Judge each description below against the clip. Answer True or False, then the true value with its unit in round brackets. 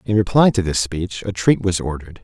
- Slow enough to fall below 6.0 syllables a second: True (5.8 syllables/s)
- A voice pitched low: True (95 Hz)